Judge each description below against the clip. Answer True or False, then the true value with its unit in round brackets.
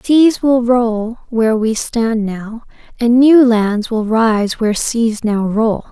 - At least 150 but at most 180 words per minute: True (160 wpm)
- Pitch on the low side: False (230 Hz)